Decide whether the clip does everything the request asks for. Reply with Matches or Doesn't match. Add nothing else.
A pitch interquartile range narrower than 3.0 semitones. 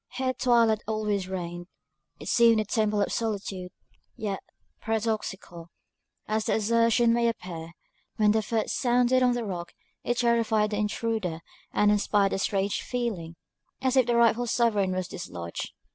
Doesn't match